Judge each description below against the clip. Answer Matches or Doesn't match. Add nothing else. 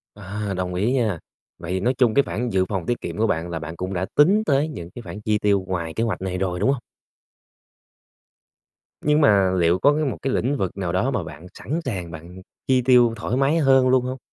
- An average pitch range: Doesn't match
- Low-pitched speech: Matches